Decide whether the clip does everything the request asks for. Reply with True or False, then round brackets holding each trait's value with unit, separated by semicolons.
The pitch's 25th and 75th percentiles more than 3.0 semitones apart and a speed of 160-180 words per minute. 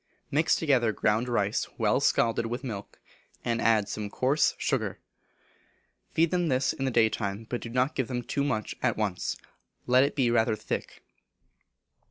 True (3.4 semitones; 170 wpm)